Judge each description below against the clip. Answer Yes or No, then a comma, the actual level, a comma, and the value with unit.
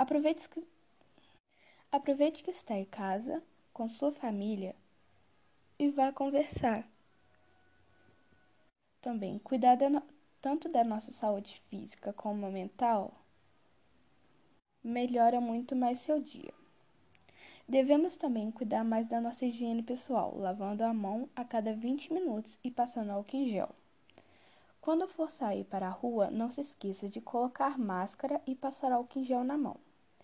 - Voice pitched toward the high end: Yes, high, 245 Hz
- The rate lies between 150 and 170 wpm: No, average, 130 wpm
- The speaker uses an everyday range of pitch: Yes, average, 4.3 semitones